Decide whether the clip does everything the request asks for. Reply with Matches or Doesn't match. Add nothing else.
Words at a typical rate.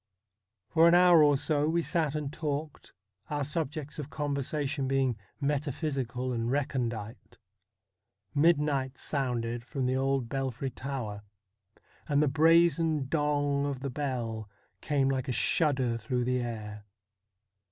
Doesn't match